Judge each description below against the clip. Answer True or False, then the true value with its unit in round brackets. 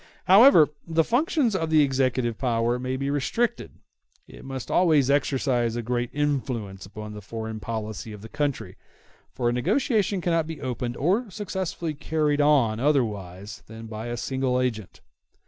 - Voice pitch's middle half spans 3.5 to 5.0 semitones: False (5.4 semitones)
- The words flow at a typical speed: True (155 wpm)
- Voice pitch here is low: True (130 Hz)